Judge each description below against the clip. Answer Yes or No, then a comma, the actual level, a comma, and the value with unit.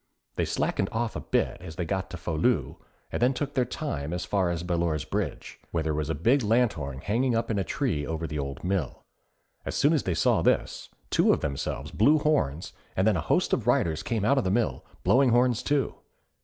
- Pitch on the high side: No, very low, 95 Hz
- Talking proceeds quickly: Yes, fast, 220 wpm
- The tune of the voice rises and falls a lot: Yes, wide, 7.2 semitones